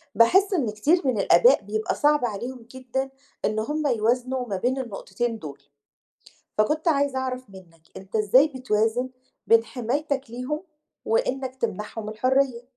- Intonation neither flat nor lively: Yes, average, 3.7 semitones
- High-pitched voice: Yes, very high, 250 Hz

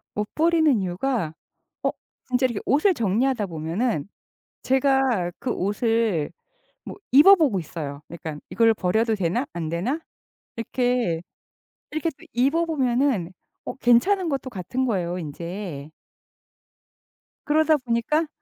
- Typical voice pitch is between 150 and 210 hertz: No, high, 235 Hz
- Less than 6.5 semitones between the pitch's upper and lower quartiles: No, wide, 7.1 semitones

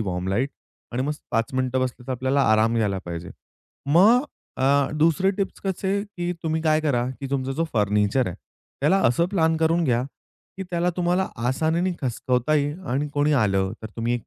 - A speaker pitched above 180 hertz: No, medium, 140 Hz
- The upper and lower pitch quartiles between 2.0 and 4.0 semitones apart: No, wide, 5.6 semitones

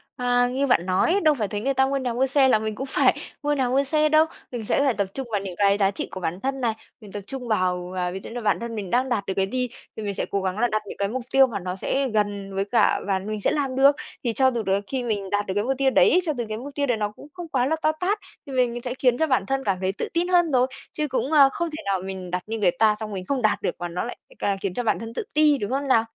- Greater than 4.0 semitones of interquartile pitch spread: Yes, average, 5.2 semitones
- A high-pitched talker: Yes, high, 240 Hz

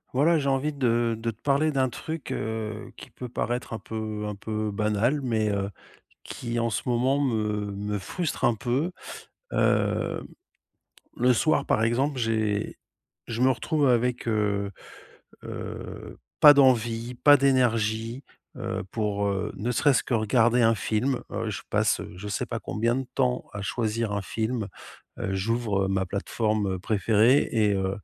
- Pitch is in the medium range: No, low, 115 Hz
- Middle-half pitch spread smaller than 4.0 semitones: Yes, average, 3.0 semitones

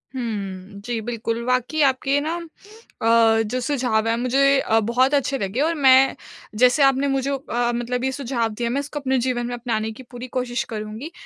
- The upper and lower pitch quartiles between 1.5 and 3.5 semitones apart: Yes, average, 2.9 semitones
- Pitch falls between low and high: No, very high, 250 Hz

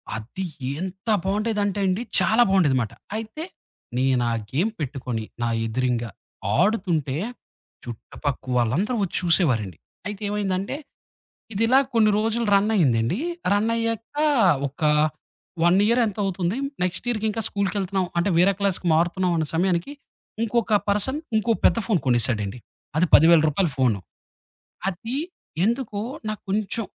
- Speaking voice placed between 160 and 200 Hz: Yes, high, 190 Hz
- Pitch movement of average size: No, wide, 7.0 semitones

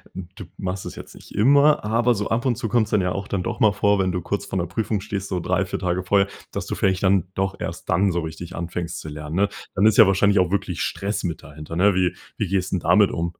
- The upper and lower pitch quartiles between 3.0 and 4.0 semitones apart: No, narrow, 2.4 semitones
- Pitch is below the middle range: Yes, very low, 95 Hz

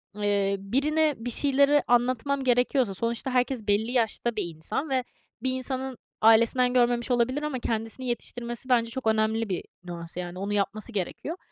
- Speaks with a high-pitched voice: Yes, high, 240 Hz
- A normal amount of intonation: Yes, average, 3.1 semitones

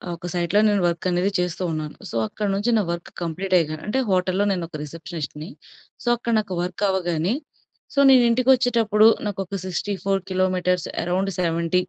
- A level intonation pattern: No, average, 3.1 semitones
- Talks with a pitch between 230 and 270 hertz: No, medium, 185 Hz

